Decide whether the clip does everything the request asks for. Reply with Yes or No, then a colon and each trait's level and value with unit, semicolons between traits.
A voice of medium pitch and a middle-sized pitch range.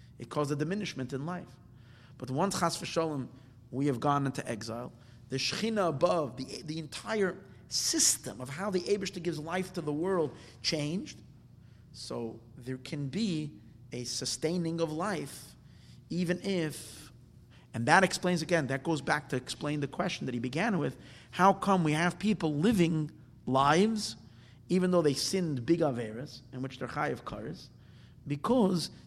No: medium, 150 Hz; wide, 5.7 semitones